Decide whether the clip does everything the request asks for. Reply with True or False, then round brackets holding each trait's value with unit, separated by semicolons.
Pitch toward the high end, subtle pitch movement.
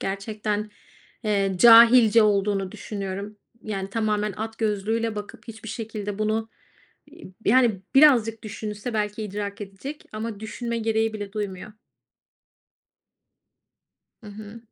True (215 Hz; 1.6 semitones)